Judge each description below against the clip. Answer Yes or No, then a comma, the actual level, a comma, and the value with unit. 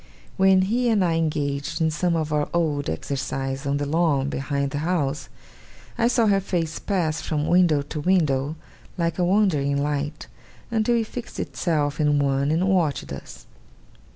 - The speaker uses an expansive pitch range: No, average, 4.4 semitones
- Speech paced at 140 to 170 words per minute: Yes, average, 165 wpm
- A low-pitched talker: No, medium, 155 Hz